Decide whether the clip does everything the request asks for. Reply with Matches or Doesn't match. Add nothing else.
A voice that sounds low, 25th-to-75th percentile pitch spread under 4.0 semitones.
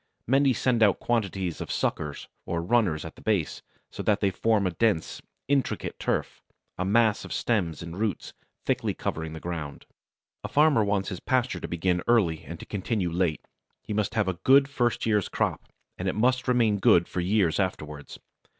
Doesn't match